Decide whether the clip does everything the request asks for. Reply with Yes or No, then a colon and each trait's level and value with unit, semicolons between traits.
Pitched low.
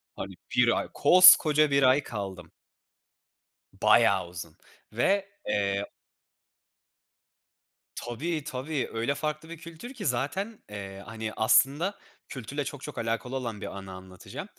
Yes: low, 130 Hz